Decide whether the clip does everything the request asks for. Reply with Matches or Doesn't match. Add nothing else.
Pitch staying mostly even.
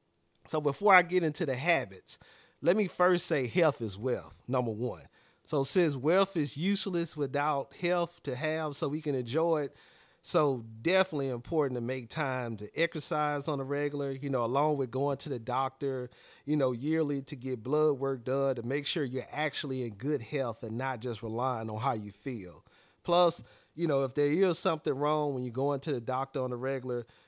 Doesn't match